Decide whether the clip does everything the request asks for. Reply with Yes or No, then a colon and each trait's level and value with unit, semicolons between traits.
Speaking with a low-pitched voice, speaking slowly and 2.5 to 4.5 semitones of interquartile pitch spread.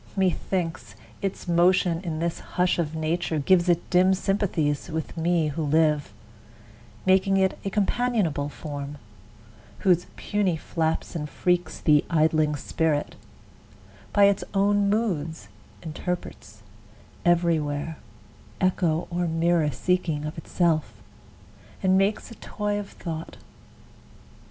No: medium, 170 Hz; slow, 120 wpm; average, 3.2 semitones